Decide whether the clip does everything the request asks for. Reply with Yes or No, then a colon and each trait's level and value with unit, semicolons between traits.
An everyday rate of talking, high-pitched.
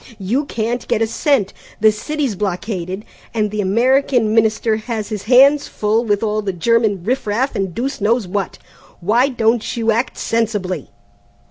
Yes: average, 160 wpm; high, 220 Hz